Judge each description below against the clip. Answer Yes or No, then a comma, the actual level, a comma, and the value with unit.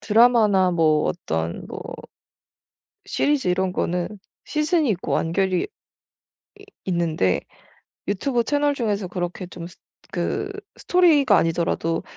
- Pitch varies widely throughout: Yes, wide, 6.2 semitones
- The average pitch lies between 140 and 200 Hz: Yes, high, 190 Hz